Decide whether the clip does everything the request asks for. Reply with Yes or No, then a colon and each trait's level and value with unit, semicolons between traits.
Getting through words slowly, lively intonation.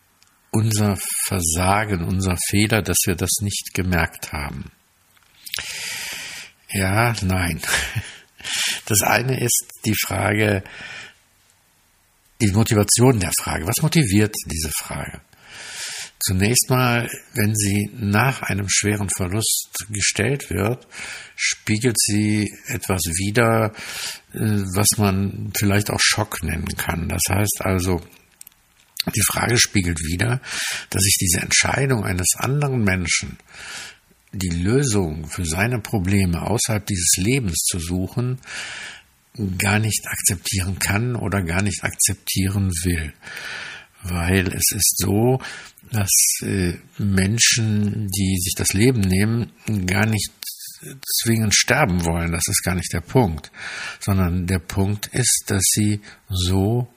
No: slow, 115 wpm; average, 2.8 semitones